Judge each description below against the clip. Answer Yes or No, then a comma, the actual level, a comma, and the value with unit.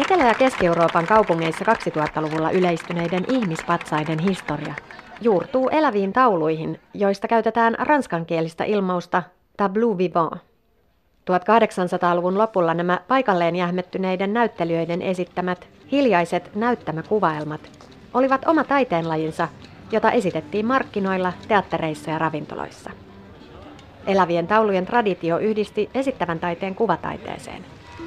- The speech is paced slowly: Yes, slow, 90 wpm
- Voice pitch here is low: No, medium, 180 Hz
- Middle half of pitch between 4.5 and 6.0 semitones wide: Yes, average, 4.8 semitones